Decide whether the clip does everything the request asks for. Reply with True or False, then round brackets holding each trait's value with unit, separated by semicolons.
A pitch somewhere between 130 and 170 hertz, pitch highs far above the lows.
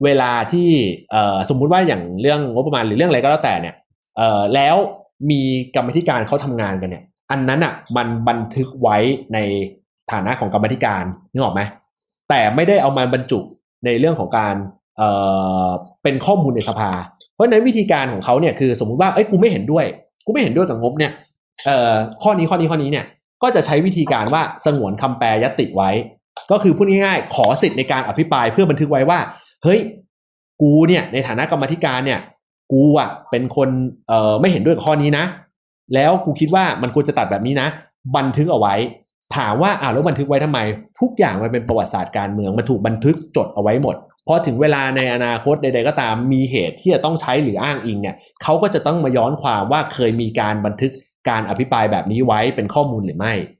True (135 Hz; 5.7 semitones)